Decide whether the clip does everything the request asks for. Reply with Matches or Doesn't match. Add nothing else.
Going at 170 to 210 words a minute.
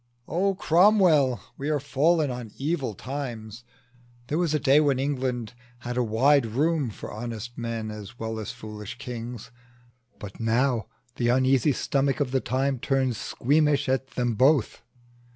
Doesn't match